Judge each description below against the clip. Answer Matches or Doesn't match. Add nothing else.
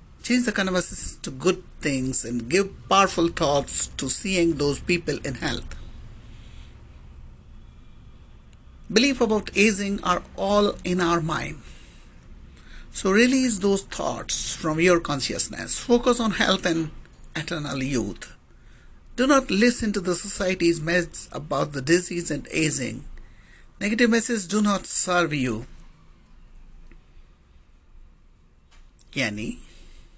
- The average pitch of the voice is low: Doesn't match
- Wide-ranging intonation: Matches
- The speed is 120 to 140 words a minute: Doesn't match